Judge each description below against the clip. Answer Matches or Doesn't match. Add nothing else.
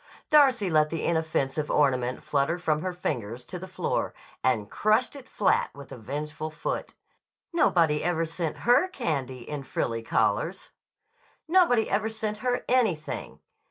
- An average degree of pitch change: Doesn't match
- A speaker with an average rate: Matches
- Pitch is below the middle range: Doesn't match